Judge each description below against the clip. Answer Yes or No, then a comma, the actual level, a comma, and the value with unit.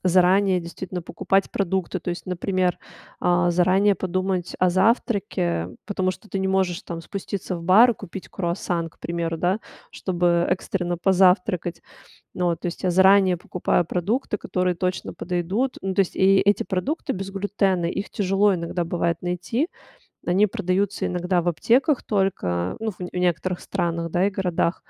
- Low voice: No, medium, 185 Hz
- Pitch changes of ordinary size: No, narrow, 1.9 semitones